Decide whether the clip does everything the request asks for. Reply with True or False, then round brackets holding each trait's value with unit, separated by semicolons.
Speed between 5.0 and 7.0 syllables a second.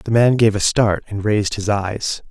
False (4.7 syllables/s)